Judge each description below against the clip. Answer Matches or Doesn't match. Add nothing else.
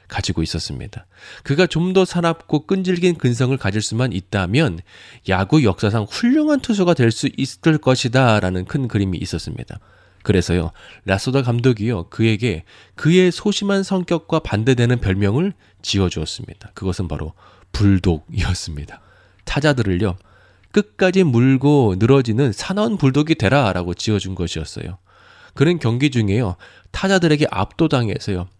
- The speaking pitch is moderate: Doesn't match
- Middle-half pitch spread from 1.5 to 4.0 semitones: Doesn't match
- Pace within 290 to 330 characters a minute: Matches